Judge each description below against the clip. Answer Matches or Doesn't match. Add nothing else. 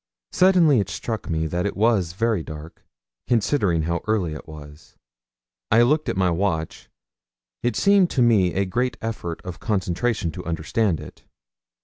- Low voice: Matches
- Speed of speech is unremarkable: Matches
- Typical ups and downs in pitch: Doesn't match